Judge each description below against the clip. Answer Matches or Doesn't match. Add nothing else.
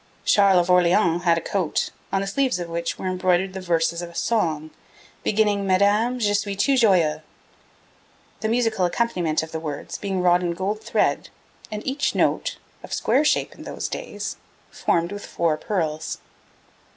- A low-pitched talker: Doesn't match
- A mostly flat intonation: Doesn't match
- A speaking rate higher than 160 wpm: Matches